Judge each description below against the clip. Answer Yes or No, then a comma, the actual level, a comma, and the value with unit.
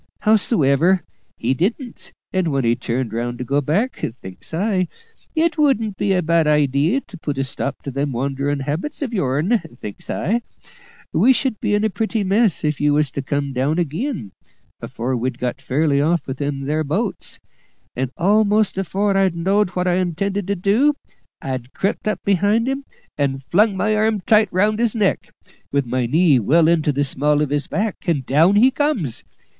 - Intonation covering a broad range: Yes, wide, 6.9 semitones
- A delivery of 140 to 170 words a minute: No, average, 185 wpm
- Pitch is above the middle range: No, medium, 170 Hz